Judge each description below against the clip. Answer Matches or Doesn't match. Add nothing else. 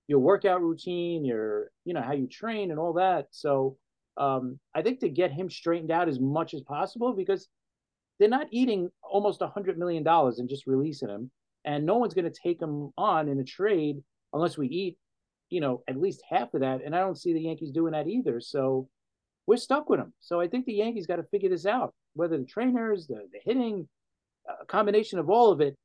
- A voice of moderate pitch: Matches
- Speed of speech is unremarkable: Doesn't match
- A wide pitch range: Matches